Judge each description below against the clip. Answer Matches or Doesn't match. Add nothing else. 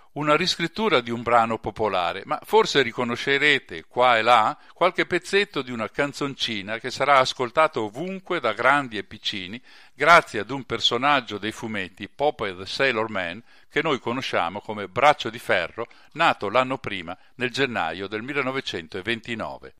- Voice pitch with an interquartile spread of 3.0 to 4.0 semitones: Doesn't match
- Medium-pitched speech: Doesn't match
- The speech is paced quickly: Doesn't match